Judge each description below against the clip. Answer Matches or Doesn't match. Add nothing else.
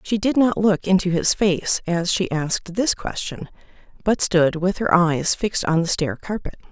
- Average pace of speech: Matches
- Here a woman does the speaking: Matches